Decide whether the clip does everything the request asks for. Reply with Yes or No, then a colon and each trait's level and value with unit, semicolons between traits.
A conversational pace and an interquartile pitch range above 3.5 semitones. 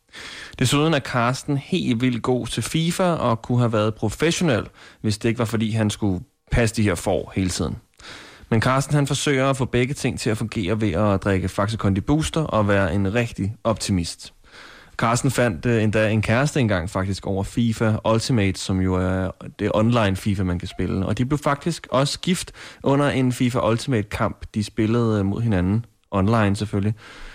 Yes: average, 180 wpm; average, 3.9 semitones